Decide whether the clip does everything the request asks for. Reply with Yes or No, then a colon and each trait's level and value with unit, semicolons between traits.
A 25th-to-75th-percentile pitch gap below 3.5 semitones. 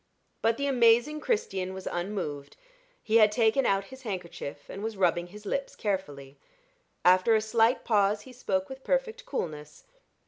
No: average, 4.7 semitones